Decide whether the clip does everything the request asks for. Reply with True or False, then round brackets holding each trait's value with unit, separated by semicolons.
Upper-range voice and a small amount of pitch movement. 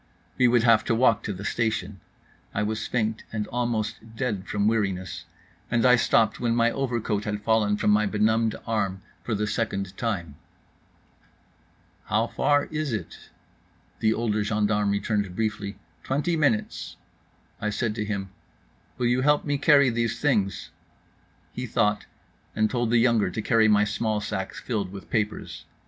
False (110 Hz; 2.2 semitones)